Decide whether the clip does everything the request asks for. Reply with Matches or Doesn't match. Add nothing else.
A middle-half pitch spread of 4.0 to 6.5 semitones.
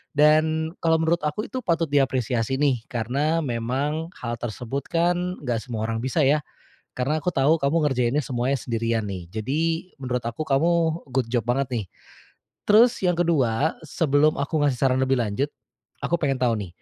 Matches